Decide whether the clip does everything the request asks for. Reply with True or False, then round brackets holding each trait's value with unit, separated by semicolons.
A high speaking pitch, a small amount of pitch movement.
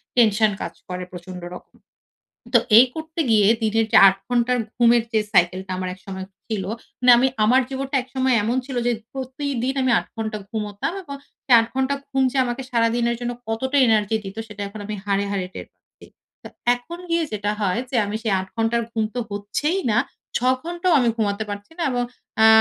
False (230 Hz; 4.1 semitones)